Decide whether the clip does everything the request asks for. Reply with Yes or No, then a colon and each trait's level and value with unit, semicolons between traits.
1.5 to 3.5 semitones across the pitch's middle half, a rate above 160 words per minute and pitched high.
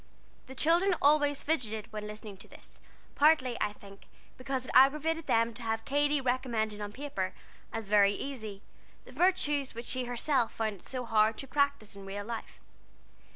No: average, 4.9 semitones; average, 170 wpm; high, 245 Hz